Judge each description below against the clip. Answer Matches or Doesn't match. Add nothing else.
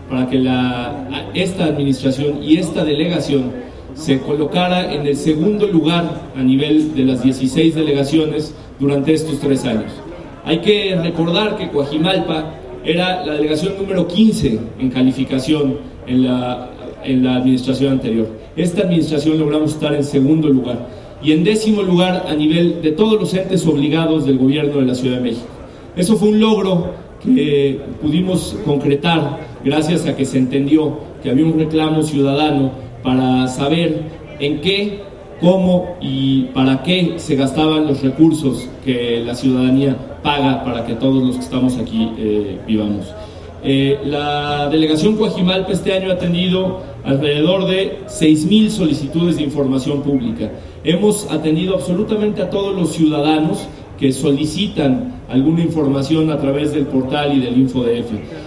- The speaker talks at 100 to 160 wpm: Matches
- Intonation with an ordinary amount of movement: Matches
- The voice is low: Doesn't match